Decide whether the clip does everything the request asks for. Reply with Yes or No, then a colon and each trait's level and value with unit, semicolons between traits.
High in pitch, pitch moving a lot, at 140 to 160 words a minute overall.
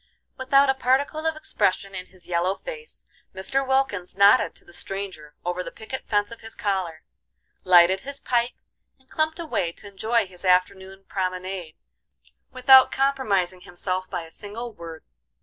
Yes: high, 200 Hz; wide, 6.2 semitones; average, 155 wpm